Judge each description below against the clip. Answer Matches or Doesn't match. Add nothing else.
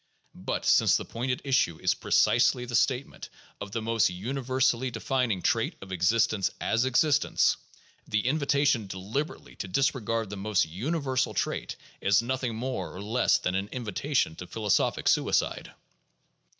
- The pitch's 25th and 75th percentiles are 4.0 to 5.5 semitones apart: Matches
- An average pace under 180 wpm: Matches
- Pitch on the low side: Matches